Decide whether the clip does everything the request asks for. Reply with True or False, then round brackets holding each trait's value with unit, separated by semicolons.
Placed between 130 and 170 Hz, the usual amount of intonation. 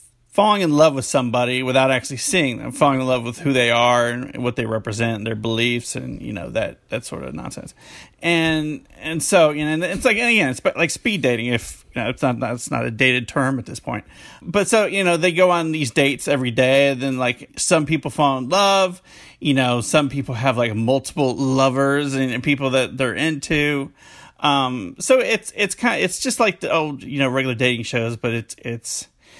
True (135 Hz; 4.4 semitones)